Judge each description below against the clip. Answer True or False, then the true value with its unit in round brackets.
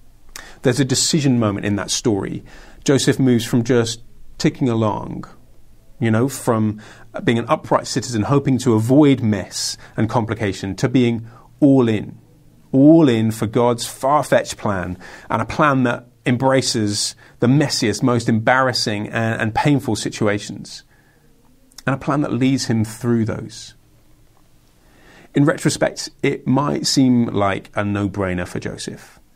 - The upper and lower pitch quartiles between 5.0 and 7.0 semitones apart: False (3.4 semitones)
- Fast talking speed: False (140 wpm)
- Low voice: True (120 Hz)